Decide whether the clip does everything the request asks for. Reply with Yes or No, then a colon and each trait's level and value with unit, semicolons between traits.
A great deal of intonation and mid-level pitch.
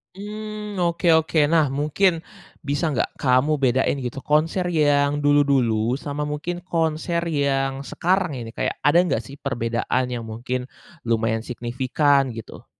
No: average, 4.3 semitones; medium, 145 Hz